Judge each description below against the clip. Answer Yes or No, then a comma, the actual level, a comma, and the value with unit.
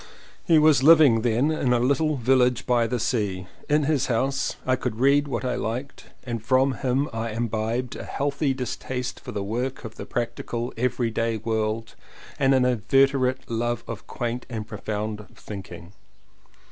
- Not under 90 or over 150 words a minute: No, average, 170 wpm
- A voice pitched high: No, low, 125 Hz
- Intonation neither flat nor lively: Yes, average, 3.0 semitones